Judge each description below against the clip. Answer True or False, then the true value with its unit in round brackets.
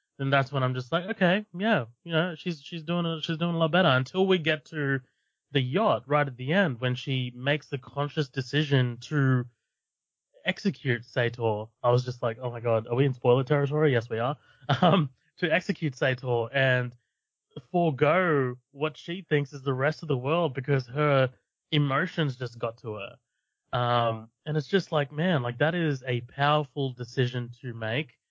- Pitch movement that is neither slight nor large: True (4.3 semitones)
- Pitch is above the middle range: False (140 Hz)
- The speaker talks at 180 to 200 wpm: True (190 wpm)